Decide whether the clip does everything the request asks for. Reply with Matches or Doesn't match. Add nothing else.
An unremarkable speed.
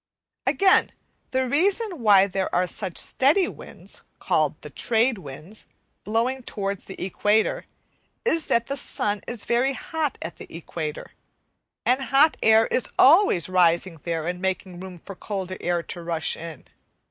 Matches